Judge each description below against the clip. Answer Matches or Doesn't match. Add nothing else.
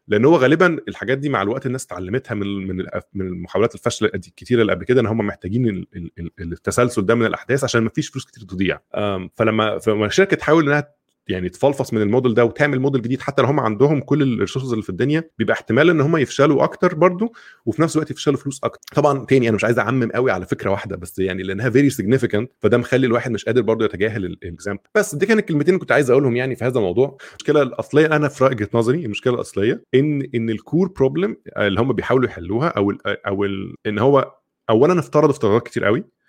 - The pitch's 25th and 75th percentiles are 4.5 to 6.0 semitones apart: Matches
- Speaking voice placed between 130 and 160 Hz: Doesn't match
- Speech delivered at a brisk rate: Matches